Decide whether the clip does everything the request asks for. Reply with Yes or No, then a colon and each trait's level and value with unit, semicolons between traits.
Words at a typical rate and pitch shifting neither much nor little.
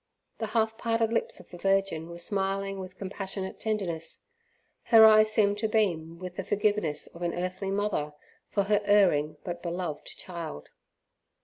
Yes: average, 155 wpm; average, 3.4 semitones